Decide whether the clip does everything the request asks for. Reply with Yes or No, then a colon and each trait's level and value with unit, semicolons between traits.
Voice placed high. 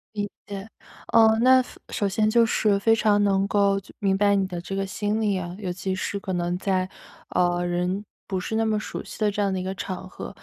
Yes: high, 195 Hz